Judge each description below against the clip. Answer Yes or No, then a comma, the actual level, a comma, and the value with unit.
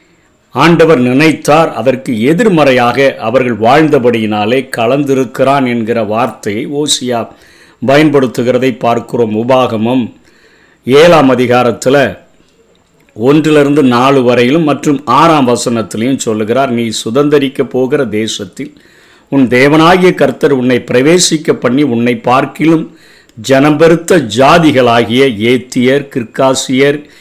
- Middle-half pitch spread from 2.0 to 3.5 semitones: Yes, average, 3.2 semitones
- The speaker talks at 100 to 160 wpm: No, average, 85 wpm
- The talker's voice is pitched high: No, low, 130 Hz